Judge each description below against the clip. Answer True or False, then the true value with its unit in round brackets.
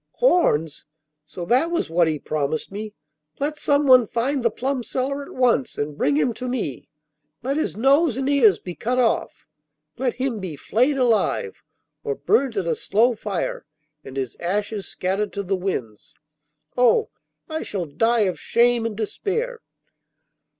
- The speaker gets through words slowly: False (160 wpm)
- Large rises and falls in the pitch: True (6.5 semitones)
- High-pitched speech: True (230 Hz)